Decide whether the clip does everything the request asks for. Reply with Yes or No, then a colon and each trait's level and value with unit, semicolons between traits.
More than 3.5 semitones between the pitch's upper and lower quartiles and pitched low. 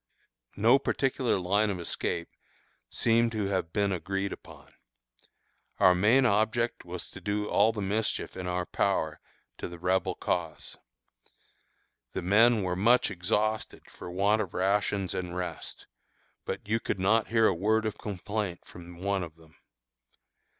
No: average, 3.2 semitones; low, 100 Hz